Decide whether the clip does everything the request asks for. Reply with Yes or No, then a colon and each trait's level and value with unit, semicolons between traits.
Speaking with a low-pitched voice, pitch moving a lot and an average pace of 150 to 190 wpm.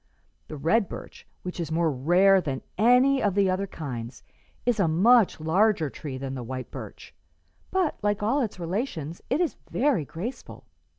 No: medium, 185 Hz; wide, 6.6 semitones; average, 170 wpm